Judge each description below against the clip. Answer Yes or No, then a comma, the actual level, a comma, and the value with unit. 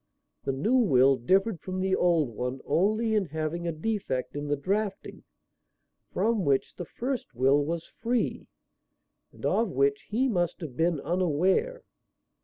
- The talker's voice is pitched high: No, medium, 175 Hz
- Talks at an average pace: Yes, average, 150 wpm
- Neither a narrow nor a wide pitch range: No, wide, 6.9 semitones